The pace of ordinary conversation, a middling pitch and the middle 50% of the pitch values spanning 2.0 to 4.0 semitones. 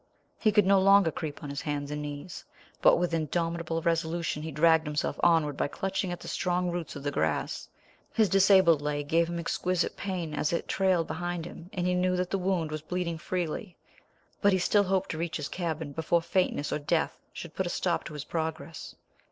No: fast, 210 wpm; medium, 170 Hz; average, 2.8 semitones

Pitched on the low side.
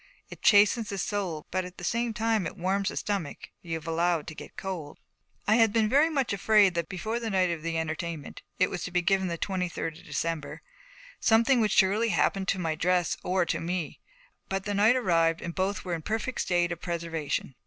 No: medium, 185 Hz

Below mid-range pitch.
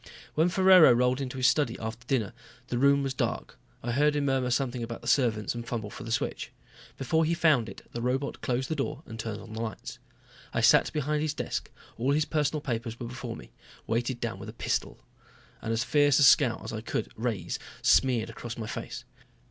Yes: low, 125 Hz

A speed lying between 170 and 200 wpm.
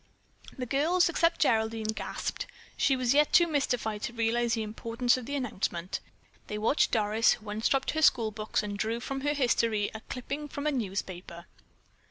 Yes: average, 175 wpm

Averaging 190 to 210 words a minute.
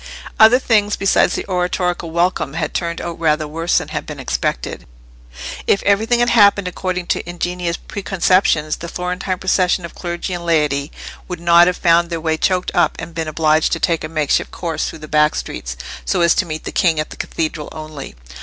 Yes: average, 195 wpm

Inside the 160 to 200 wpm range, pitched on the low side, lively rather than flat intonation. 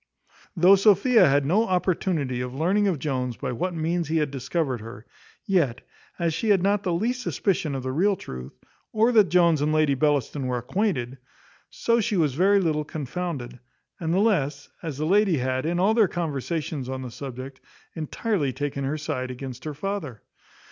No: average, 180 wpm; medium, 155 Hz; wide, 6.0 semitones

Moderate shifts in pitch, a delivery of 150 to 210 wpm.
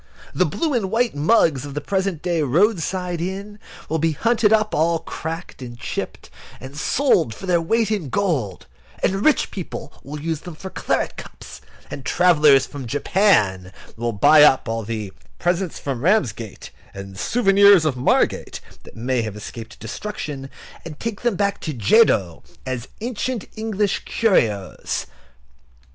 No: wide, 7.8 semitones; average, 155 wpm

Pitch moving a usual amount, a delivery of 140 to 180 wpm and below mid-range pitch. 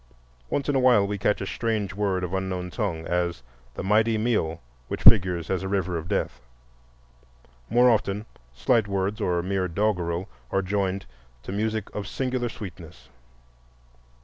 Yes: average, 3.2 semitones; average, 160 wpm; low, 100 Hz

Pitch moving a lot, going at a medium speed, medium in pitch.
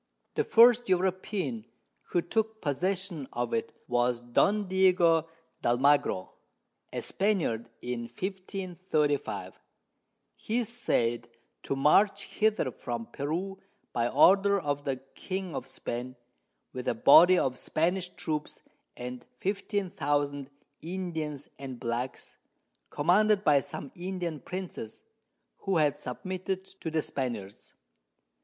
No: wide, 6.7 semitones; slow, 110 wpm; medium, 160 Hz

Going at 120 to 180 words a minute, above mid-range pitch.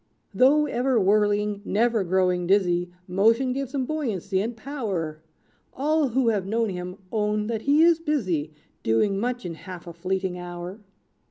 Yes: average, 155 wpm; high, 210 Hz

